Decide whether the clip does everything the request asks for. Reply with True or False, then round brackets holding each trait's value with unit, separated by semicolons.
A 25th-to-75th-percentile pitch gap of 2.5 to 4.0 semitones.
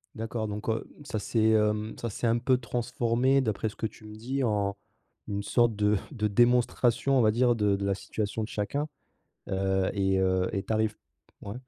True (2.8 semitones)